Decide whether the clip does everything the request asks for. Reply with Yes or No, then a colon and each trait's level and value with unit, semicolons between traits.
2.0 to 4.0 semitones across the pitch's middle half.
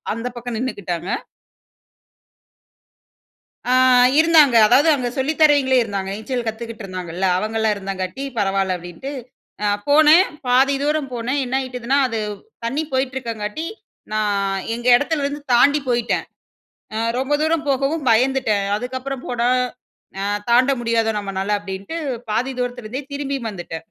No: average, 4.7 semitones